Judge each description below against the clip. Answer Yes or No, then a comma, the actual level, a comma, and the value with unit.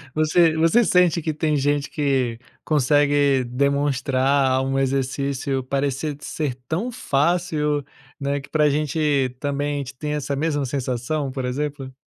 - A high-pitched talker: No, medium, 145 Hz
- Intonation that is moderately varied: No, narrow, 2.0 semitones